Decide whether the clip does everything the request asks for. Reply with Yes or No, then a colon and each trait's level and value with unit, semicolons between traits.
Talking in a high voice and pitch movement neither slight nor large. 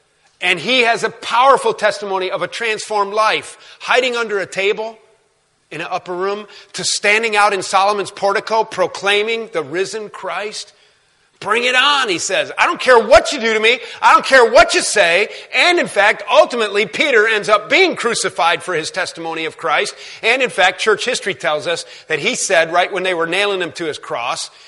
Yes: high, 210 Hz; average, 3.4 semitones